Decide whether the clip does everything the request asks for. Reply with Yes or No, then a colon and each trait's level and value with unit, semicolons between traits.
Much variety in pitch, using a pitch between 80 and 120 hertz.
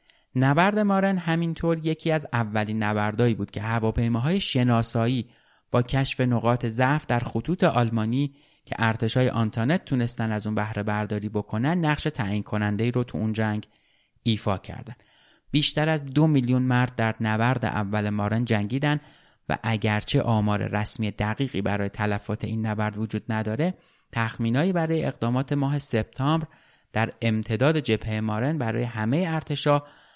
No: average, 4.7 semitones; low, 115 Hz